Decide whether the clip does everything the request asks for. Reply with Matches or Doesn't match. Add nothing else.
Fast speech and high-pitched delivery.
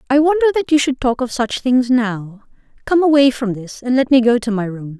Matches